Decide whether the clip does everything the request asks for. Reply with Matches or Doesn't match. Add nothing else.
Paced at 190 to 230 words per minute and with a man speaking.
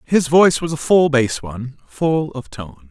Matches